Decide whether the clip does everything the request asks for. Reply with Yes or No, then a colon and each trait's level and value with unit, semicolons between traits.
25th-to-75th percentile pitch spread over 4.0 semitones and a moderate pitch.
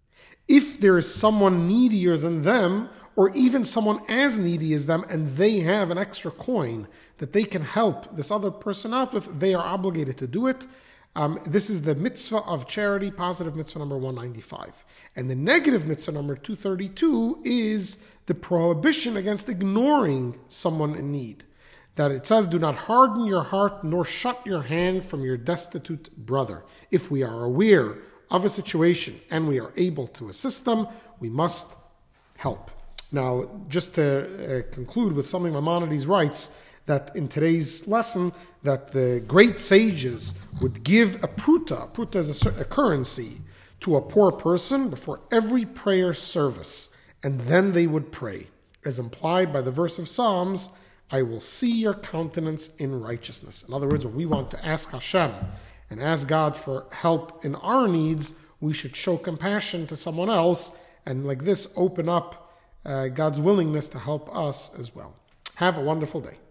Yes: wide, 5.6 semitones; medium, 170 Hz